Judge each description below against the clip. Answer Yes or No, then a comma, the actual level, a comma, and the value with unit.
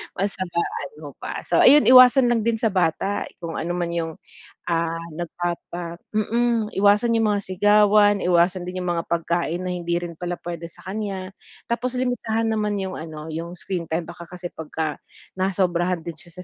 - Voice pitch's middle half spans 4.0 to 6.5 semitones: No, average, 3.5 semitones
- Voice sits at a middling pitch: Yes, medium, 180 Hz